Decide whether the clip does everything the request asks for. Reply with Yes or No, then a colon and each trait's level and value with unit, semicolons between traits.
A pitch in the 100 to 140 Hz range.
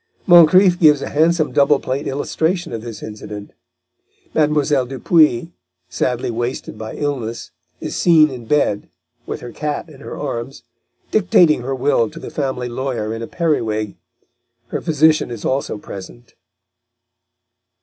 Yes: low, 135 Hz